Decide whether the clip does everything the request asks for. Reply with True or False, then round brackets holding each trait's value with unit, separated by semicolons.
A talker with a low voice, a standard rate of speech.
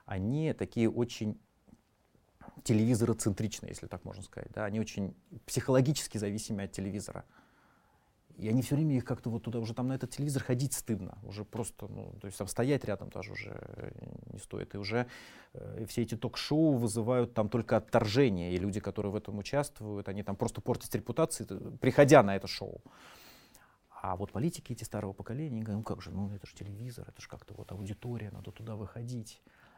False (115 Hz; 180 wpm)